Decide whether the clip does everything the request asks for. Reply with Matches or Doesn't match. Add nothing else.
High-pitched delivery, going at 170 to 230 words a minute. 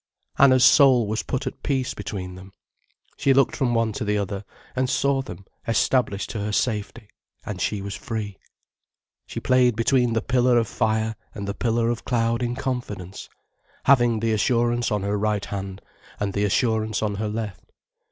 Doesn't match